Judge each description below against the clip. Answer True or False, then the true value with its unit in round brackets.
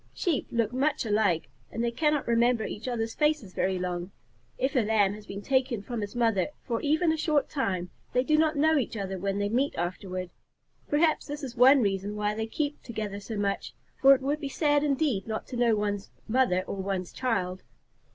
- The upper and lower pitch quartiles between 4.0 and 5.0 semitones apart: False (5.5 semitones)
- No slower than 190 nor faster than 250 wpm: True (205 wpm)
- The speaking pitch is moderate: False (230 Hz)